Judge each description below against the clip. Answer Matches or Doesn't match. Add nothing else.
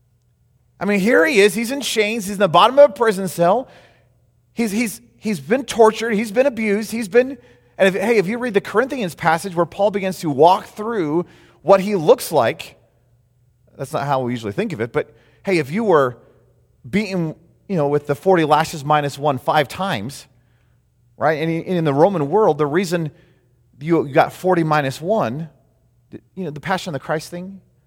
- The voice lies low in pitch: Doesn't match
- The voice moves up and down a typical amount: Doesn't match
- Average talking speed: Matches